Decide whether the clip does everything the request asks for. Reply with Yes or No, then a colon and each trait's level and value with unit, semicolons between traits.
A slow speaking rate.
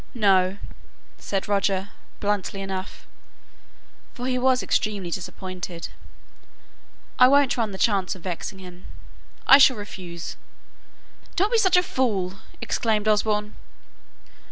Yes: slow, 115 wpm